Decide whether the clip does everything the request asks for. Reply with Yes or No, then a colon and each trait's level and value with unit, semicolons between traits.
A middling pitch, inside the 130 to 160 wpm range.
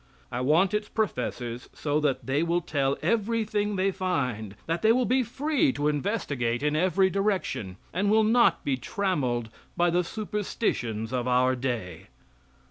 Yes: medium, 170 Hz; average, 155 wpm